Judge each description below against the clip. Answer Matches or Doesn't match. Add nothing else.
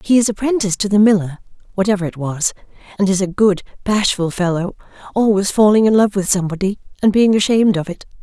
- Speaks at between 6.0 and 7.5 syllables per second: Matches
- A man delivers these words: Doesn't match